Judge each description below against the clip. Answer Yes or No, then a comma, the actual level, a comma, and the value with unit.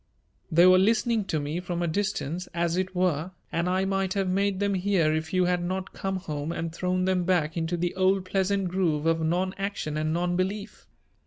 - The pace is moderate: No, fast, 210 wpm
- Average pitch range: No, narrow, 2.2 semitones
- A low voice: No, medium, 180 Hz